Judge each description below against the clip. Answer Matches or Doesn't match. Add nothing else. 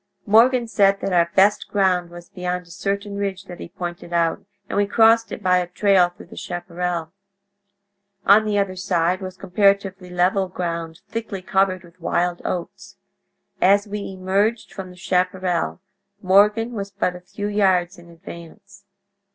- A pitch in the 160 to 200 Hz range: Matches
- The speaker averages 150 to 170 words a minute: Matches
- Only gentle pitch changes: Matches